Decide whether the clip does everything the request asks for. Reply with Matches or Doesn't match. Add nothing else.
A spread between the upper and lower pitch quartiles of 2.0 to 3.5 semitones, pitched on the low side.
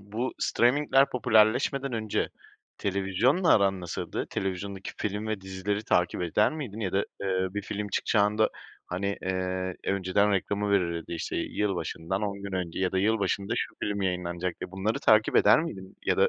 Matches